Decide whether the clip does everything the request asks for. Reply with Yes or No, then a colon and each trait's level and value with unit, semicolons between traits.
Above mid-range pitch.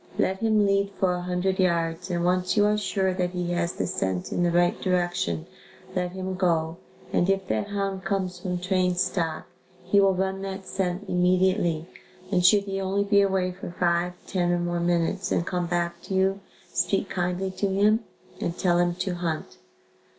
No: medium, 180 Hz